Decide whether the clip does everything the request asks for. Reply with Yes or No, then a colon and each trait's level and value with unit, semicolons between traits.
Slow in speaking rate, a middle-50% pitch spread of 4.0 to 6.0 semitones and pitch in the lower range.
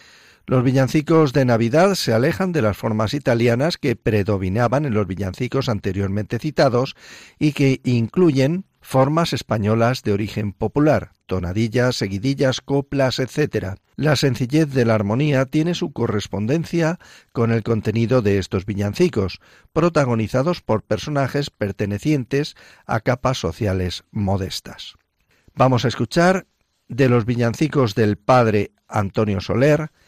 Yes: slow, 120 wpm; average, 5.1 semitones; low, 120 Hz